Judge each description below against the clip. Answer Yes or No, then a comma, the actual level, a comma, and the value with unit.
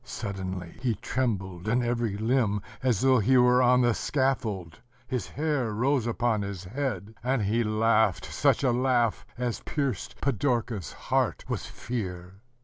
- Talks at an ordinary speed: Yes, average, 145 wpm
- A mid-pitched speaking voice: No, low, 115 Hz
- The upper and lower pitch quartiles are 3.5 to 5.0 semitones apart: Yes, average, 3.9 semitones